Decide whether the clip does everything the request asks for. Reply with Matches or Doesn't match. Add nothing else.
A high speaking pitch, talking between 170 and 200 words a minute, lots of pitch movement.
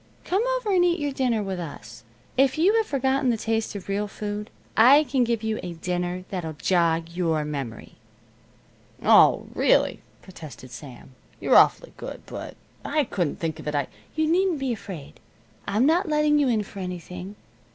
Matches